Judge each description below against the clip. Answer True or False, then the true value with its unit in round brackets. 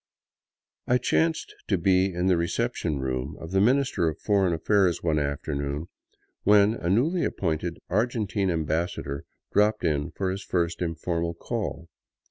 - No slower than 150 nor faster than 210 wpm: False (140 wpm)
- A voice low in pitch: True (90 Hz)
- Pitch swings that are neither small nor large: True (4.2 semitones)